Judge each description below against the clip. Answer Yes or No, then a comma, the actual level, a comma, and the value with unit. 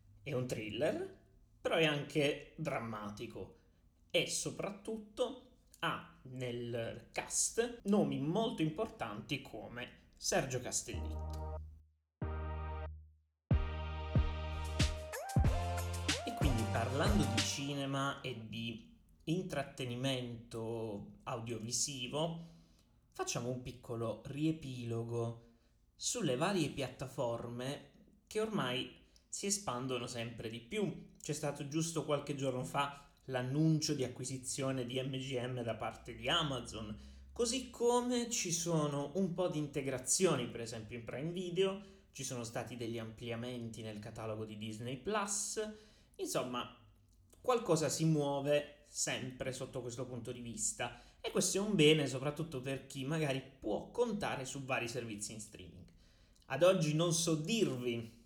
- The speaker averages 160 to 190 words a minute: No, slow, 115 wpm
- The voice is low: Yes, low, 130 Hz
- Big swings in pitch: Yes, wide, 5.8 semitones